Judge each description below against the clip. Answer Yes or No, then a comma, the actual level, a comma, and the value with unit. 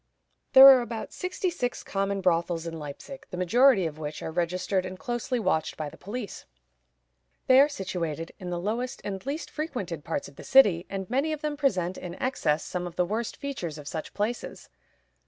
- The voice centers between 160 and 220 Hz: Yes, high, 190 Hz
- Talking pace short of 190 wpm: No, average, 195 wpm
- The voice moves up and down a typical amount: No, wide, 6.9 semitones